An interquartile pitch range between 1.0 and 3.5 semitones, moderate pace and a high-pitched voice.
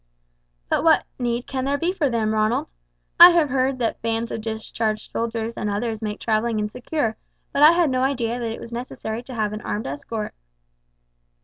Yes: average, 3.1 semitones; average, 190 wpm; high, 230 Hz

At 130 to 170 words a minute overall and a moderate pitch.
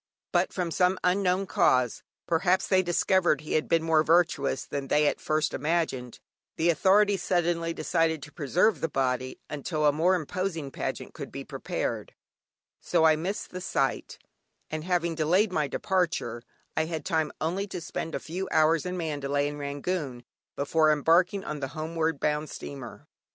Yes: average, 165 wpm; medium, 160 Hz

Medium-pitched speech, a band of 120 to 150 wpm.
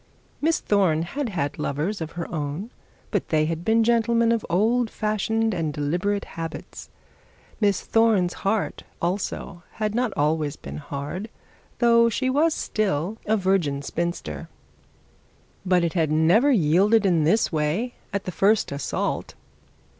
No: high, 195 Hz; average, 140 wpm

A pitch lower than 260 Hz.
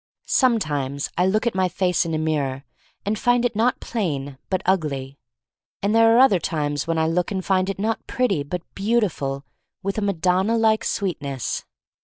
Yes: medium, 185 Hz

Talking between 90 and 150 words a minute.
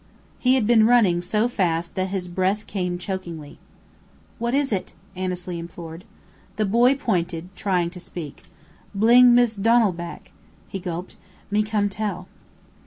Yes: average, 145 wpm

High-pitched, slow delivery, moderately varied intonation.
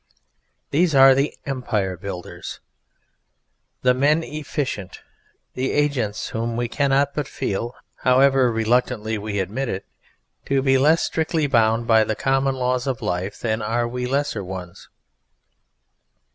No: low, 125 Hz; slow, 130 wpm; average, 3.9 semitones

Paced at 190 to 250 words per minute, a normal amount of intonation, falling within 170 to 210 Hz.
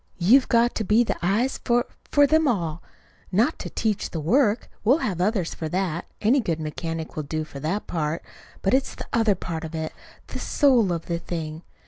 No: average, 200 wpm; wide, 6.5 semitones; high, 190 Hz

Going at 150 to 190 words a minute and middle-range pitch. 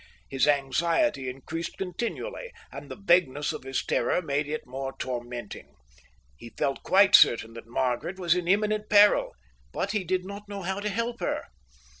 Yes: average, 165 wpm; medium, 170 Hz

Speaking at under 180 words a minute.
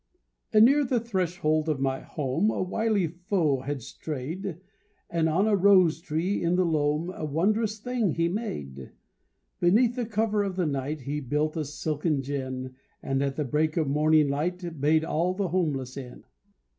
Yes: average, 170 wpm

